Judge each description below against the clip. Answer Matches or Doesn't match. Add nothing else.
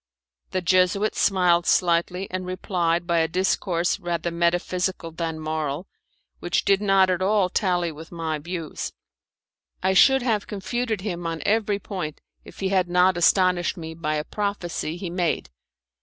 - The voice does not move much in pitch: Matches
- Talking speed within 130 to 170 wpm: Matches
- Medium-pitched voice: Matches